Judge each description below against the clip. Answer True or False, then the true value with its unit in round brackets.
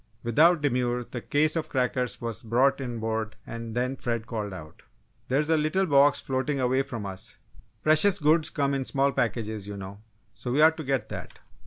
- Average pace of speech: True (185 wpm)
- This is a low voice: True (130 Hz)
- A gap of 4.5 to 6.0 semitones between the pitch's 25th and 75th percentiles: False (4.1 semitones)